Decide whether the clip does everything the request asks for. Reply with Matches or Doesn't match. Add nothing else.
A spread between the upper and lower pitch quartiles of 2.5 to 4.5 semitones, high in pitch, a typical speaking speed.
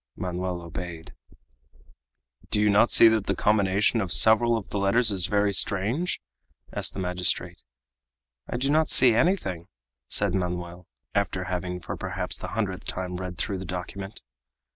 Doesn't match